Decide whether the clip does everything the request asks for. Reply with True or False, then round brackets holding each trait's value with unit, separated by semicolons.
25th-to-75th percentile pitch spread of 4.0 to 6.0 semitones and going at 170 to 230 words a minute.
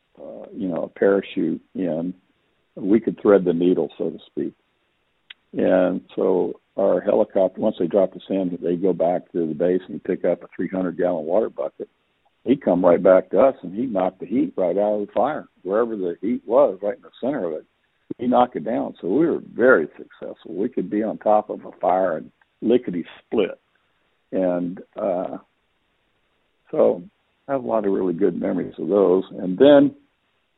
False (3.6 semitones; 190 wpm)